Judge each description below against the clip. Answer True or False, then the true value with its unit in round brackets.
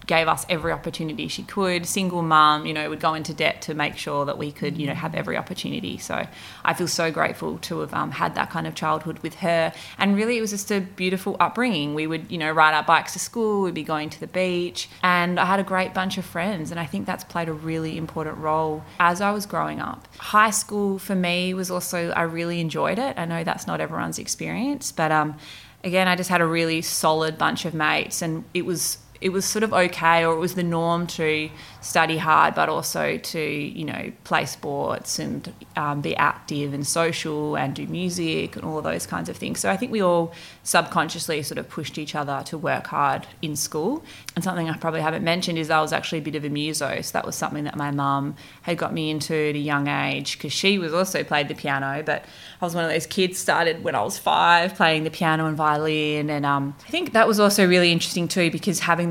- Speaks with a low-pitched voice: False (165 Hz)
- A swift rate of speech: True (240 wpm)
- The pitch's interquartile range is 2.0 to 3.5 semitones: True (2.7 semitones)